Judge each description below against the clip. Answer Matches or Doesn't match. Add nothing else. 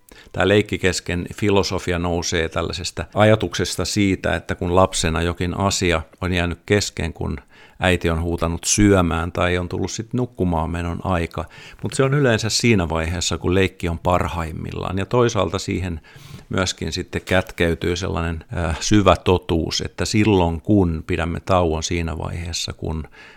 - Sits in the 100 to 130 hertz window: Doesn't match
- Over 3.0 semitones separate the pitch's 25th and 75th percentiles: Doesn't match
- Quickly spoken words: Doesn't match